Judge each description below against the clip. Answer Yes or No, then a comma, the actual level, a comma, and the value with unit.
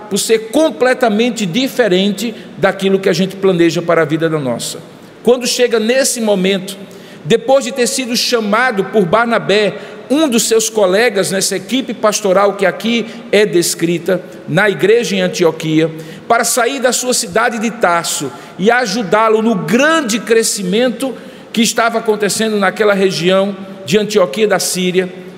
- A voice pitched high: Yes, high, 210 Hz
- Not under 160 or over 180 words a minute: No, average, 145 wpm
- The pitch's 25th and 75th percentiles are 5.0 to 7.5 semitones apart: No, average, 3.8 semitones